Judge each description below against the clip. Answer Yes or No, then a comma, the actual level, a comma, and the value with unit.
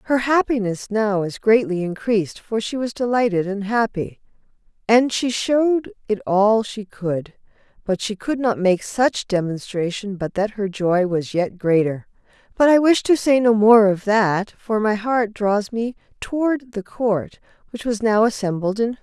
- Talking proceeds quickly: No, average, 175 wpm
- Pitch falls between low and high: No, high, 215 Hz